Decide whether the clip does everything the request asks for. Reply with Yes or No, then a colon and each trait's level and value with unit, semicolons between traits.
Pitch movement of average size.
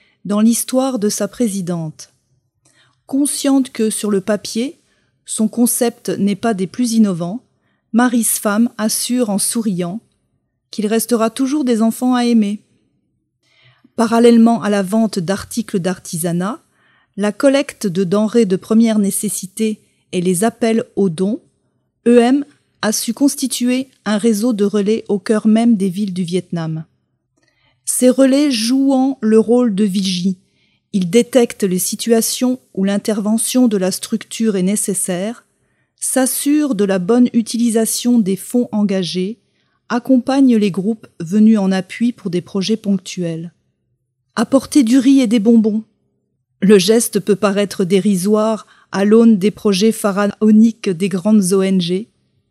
Yes: average, 3.3 semitones